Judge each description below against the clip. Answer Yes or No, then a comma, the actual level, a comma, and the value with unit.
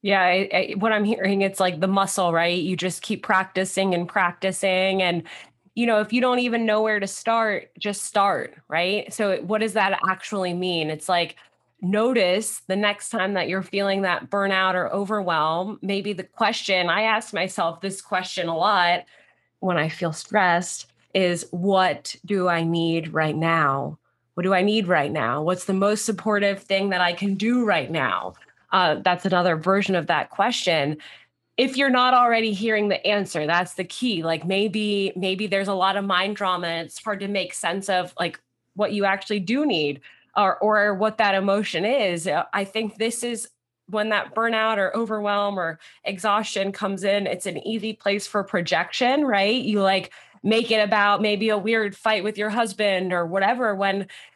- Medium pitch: No, high, 195 Hz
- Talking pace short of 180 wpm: No, average, 185 wpm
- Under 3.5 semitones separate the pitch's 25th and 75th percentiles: Yes, average, 2.8 semitones